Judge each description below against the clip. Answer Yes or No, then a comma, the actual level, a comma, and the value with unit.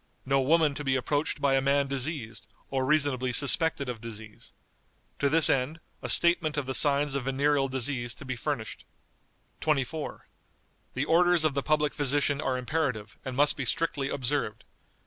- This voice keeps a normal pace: Yes, average, 165 wpm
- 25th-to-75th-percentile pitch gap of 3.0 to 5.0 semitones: No, narrow, 2.4 semitones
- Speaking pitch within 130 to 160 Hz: Yes, medium, 140 Hz